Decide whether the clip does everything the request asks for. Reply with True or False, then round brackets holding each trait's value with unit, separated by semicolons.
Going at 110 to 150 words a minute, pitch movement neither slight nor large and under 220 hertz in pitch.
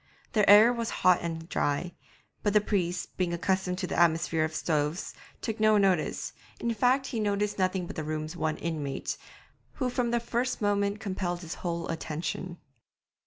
False (170 wpm; 4.2 semitones; 185 Hz)